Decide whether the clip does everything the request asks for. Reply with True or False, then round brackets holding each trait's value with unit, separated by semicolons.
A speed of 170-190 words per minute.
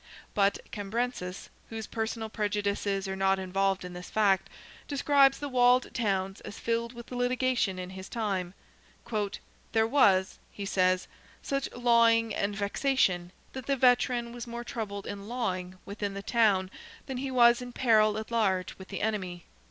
False (155 wpm)